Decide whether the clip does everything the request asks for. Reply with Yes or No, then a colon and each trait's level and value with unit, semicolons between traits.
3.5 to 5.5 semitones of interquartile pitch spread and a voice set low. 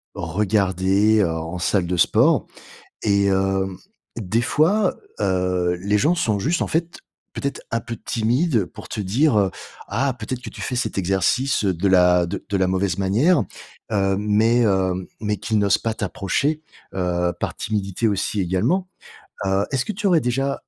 Yes: average, 4.5 semitones; low, 100 Hz